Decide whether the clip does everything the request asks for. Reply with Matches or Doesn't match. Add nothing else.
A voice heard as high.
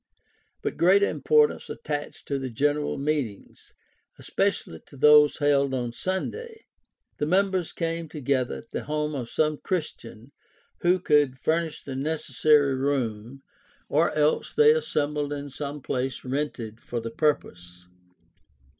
Doesn't match